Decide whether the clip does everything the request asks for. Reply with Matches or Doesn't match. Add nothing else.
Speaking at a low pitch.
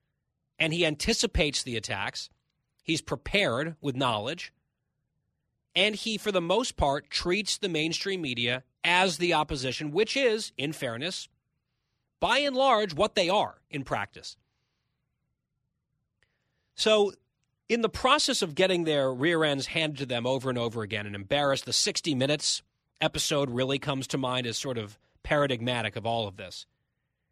Doesn't match